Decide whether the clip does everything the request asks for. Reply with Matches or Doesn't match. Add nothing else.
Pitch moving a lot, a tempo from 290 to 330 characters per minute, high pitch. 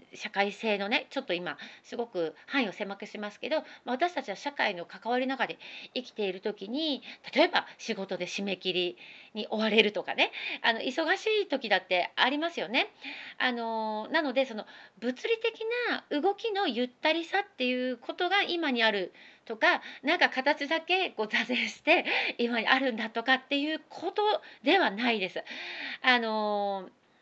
Matches